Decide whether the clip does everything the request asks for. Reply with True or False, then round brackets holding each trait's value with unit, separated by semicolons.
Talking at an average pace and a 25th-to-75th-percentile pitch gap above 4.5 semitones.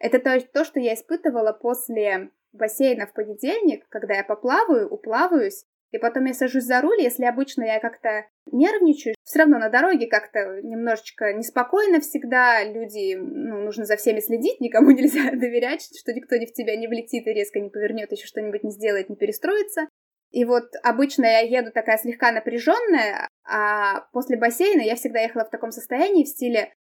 False (170 wpm; 4.9 semitones)